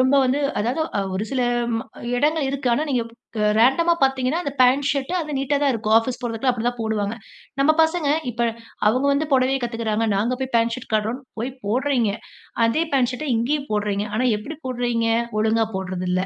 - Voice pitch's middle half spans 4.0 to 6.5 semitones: No, average, 3.5 semitones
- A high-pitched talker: Yes, very high, 250 Hz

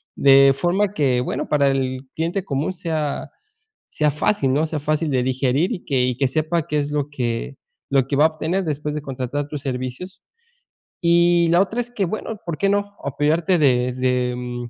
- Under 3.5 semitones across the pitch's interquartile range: No, average, 4.6 semitones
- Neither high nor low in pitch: Yes, medium, 145 Hz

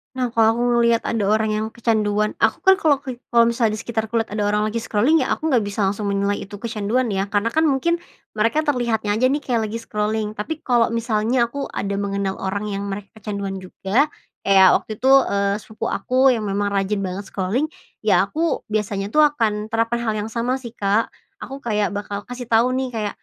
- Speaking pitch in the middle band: No, high, 220 Hz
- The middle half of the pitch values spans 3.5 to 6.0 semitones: No, average, 3.1 semitones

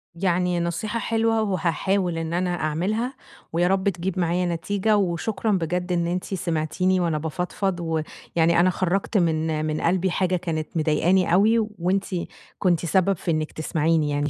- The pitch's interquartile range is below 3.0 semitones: Yes, narrow, 2.6 semitones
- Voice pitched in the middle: Yes, medium, 175 Hz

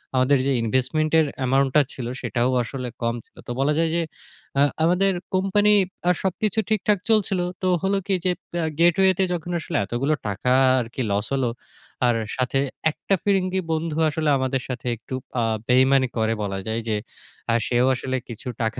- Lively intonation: Yes, wide, 6.6 semitones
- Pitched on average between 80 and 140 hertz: Yes, low, 135 Hz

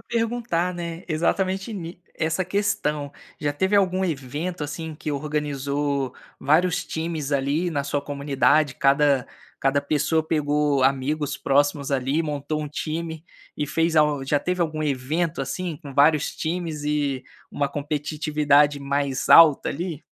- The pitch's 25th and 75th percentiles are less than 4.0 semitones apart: Yes, average, 2.7 semitones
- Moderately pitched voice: Yes, medium, 150 Hz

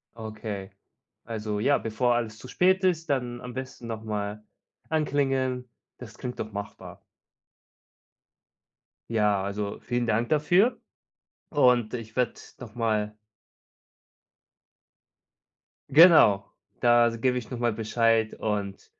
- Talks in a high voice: No, low, 115 Hz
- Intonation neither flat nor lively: Yes, average, 3.1 semitones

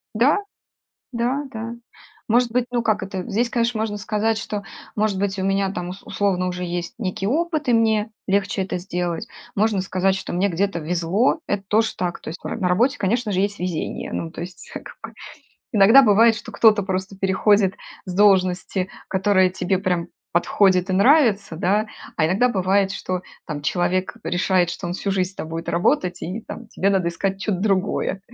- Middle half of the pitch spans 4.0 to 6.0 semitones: No, average, 3.0 semitones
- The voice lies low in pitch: No, high, 195 Hz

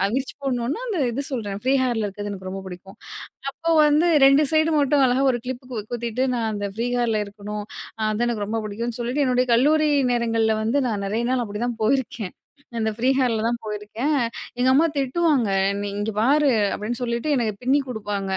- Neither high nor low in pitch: No, high, 235 Hz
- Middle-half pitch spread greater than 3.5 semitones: Yes, average, 3.9 semitones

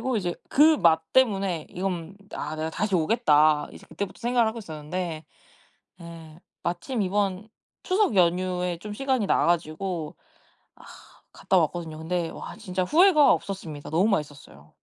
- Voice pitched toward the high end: No, medium, 180 Hz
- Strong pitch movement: No, average, 4.5 semitones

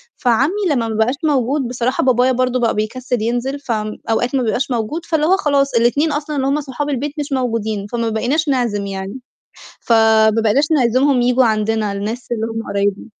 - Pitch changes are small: No, average, 3.8 semitones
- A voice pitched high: Yes, high, 245 Hz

